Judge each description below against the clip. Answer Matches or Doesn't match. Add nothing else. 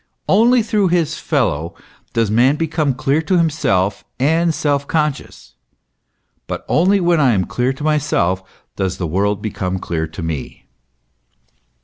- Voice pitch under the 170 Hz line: Matches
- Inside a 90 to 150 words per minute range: Matches